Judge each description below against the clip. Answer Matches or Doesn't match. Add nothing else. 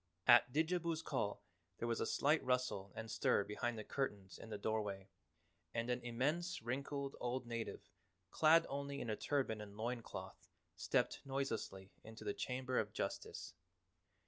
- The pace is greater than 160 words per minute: Doesn't match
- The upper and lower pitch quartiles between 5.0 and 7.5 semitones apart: Doesn't match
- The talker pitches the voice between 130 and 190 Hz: Doesn't match